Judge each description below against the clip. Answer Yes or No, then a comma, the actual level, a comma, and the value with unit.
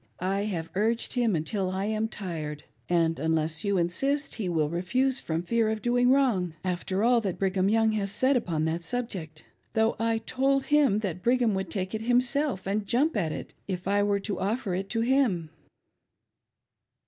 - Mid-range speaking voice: No, high, 200 Hz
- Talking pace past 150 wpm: Yes, average, 185 wpm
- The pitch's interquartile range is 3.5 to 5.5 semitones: Yes, average, 5.0 semitones